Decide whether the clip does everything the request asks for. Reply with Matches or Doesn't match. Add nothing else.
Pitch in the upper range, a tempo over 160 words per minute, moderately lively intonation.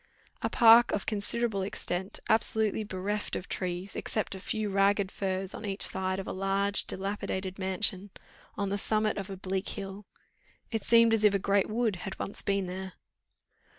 Doesn't match